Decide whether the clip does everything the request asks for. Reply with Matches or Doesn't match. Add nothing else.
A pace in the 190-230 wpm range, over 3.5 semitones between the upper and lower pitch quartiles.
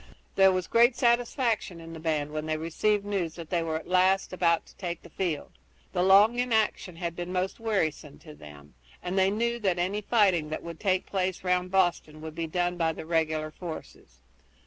Doesn't match